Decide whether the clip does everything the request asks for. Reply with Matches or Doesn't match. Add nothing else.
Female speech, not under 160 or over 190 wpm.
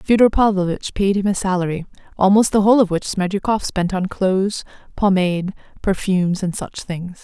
Matches